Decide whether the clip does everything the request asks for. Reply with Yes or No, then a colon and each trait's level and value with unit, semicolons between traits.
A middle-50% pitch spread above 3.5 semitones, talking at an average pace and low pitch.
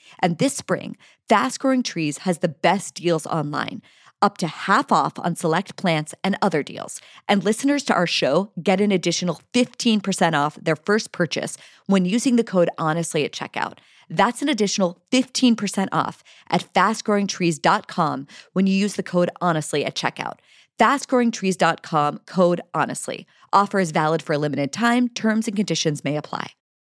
No: average, 4.4 semitones; average, 160 wpm; medium, 185 Hz